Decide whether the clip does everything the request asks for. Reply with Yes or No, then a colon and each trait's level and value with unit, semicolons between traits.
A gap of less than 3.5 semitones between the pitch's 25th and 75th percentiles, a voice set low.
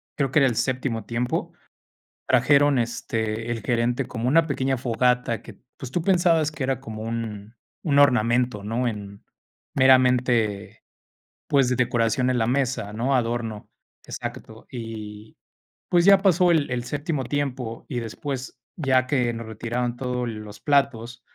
Yes: average, 3.0 semitones; low, 125 Hz